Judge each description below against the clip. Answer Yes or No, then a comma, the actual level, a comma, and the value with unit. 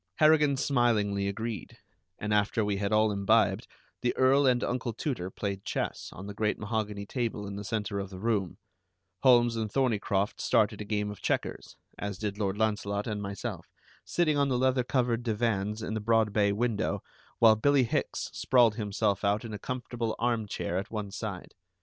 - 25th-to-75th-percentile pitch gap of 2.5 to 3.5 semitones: Yes, average, 3.0 semitones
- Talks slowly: No, average, 180 wpm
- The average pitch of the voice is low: Yes, low, 110 Hz